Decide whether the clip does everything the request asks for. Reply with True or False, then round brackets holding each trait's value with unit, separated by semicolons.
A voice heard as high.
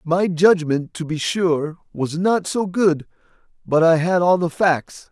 False (170 Hz)